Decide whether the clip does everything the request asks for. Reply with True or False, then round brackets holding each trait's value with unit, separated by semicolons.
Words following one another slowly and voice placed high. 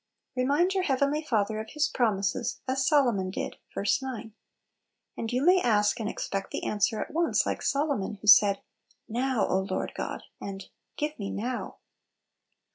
False (170 wpm; 235 Hz)